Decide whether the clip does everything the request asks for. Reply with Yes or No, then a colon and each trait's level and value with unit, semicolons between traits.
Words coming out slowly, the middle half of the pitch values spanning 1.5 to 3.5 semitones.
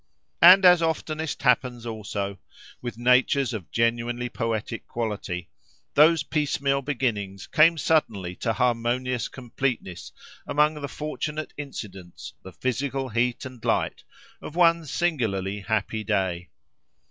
No: slow, 115 wpm; average, 5.1 semitones